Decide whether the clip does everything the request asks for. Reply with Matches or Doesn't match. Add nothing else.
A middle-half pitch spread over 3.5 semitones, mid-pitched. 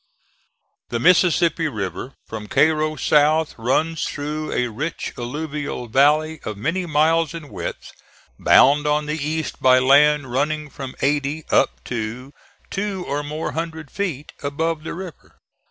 Doesn't match